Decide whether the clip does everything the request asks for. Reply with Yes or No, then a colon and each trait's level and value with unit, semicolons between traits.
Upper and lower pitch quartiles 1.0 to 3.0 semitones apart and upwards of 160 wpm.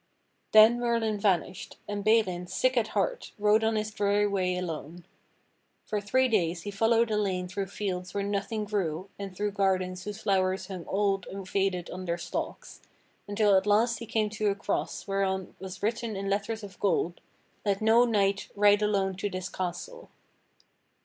Yes: narrow, 2.4 semitones; average, 175 wpm